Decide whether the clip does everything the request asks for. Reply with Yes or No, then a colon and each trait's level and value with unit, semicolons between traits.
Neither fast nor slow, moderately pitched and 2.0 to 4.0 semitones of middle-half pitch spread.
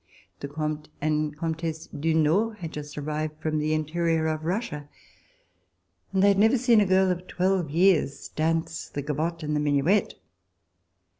Yes: average, 165 wpm; medium, 160 Hz; average, 3.2 semitones